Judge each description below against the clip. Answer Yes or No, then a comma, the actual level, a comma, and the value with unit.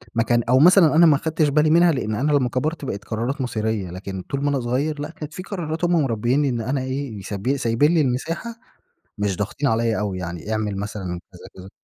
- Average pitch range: No, wide, 5.7 semitones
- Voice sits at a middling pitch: No, low, 130 Hz